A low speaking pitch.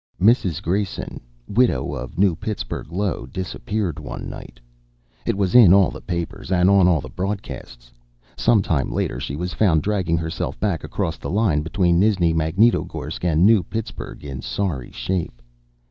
Yes: very low, 90 Hz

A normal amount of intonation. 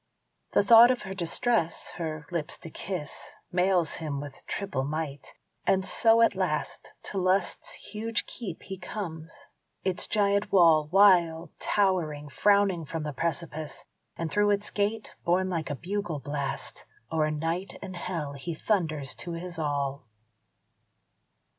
Yes: average, 4.3 semitones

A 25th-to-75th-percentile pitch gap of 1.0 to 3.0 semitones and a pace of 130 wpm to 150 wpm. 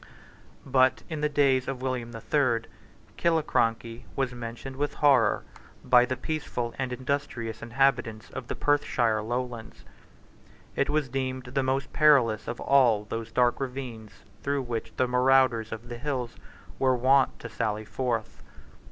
Yes: narrow, 2.6 semitones; average, 145 wpm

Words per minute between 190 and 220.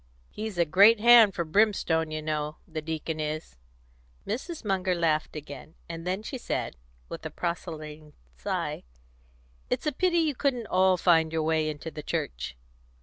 No: average, 160 wpm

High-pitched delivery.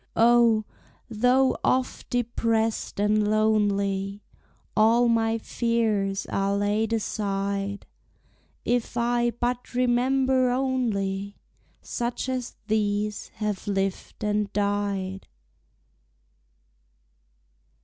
Yes: high, 220 Hz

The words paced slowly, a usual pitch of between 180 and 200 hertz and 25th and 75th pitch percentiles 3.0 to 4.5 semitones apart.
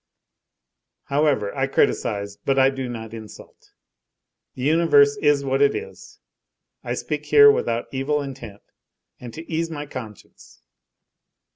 No: slow, 130 wpm; low, 135 Hz; average, 4.1 semitones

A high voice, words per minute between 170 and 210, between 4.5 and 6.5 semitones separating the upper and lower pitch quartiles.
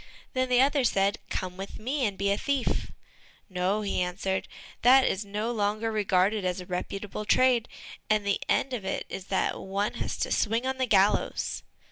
No: high, 205 Hz; average, 185 wpm; average, 4.0 semitones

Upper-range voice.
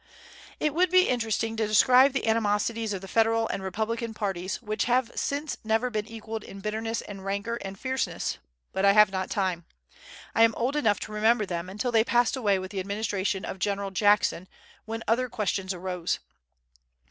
Yes: high, 215 Hz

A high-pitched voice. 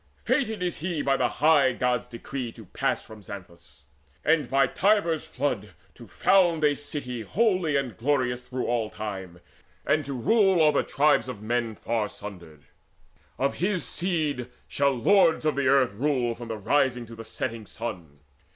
No: low, 125 Hz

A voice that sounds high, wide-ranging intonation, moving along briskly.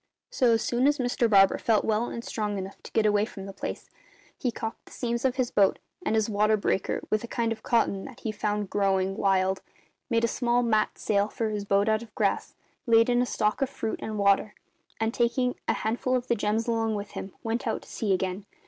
No: high, 220 Hz; narrow, 2.6 semitones; fast, 230 wpm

